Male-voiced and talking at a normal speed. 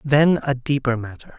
Yes: male; average, 175 wpm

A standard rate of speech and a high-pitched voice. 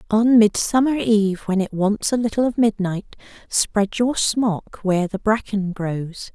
Yes: average, 160 wpm; high, 210 Hz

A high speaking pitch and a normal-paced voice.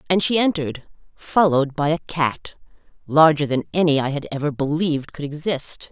No: medium, 150 Hz; average, 160 wpm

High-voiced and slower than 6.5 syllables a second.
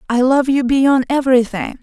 Yes: very high, 260 Hz; 5.0 syllables/s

